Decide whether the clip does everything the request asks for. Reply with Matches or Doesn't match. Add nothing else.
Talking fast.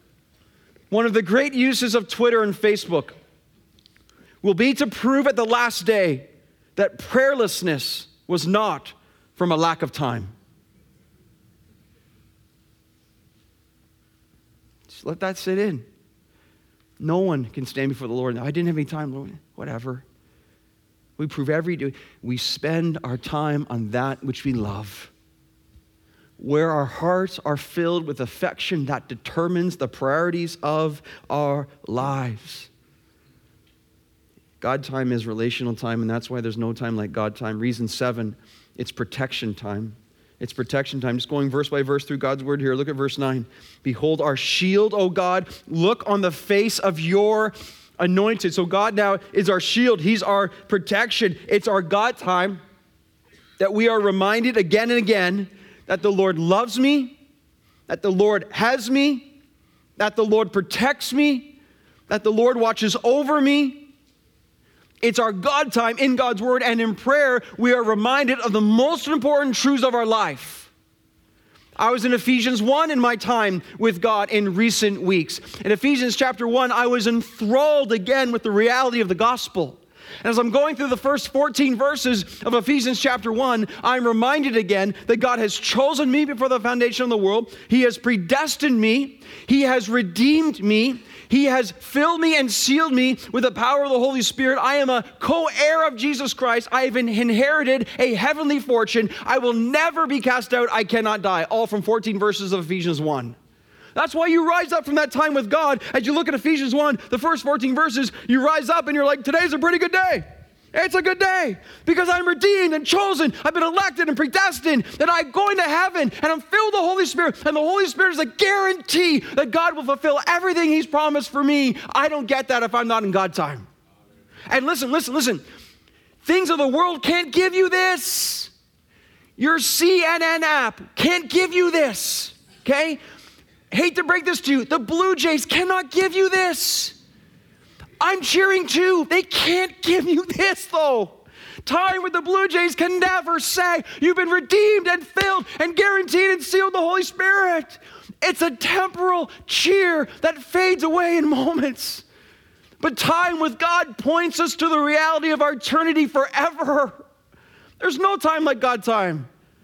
Doesn't match